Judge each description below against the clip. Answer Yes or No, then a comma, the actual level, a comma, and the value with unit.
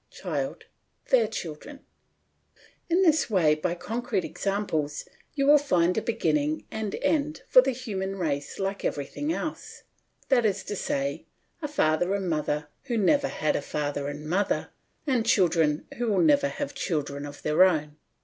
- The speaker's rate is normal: Yes, average, 160 wpm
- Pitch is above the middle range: Yes, high, 195 Hz